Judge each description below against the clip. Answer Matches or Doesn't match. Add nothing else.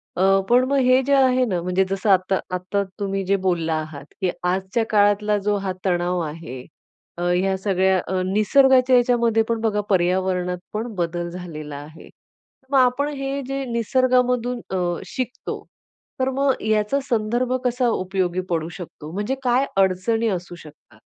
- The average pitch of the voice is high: Matches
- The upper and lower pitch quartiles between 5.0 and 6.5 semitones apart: Matches